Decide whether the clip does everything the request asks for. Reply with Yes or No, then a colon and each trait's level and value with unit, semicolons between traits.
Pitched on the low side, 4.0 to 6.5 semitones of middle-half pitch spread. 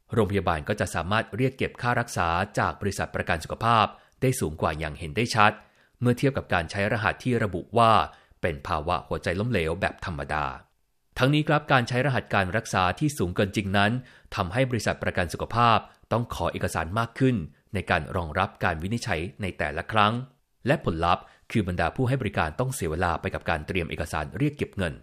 Yes: low, 100 Hz; average, 5.1 semitones